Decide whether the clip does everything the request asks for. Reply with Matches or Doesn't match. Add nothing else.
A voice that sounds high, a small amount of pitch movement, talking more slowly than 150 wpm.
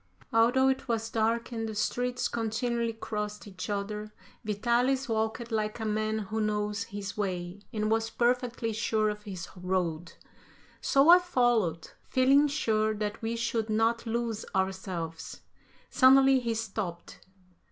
Matches